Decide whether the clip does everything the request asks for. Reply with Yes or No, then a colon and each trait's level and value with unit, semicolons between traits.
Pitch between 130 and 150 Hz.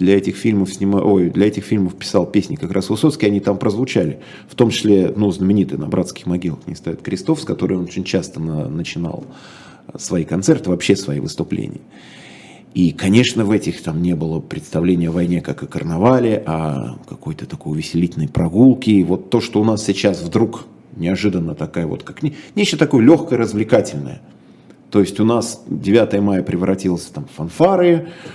No: low, 100 Hz